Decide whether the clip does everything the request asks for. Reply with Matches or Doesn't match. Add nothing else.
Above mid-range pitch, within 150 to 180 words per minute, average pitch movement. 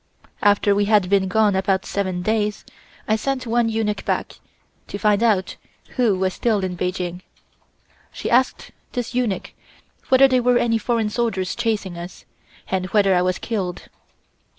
Matches